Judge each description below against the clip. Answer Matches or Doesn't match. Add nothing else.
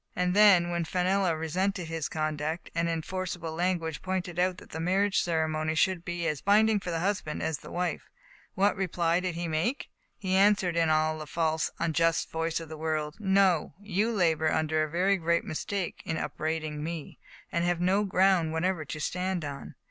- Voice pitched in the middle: Matches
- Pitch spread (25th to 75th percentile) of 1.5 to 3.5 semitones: Matches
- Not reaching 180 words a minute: Doesn't match